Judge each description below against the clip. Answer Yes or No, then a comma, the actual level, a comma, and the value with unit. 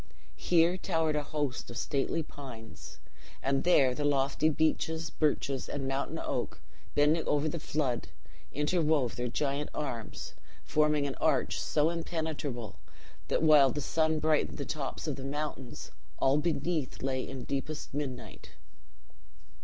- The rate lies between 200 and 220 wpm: No, average, 140 wpm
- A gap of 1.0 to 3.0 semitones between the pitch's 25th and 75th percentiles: Yes, narrow, 2.6 semitones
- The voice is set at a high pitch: No, medium, 145 Hz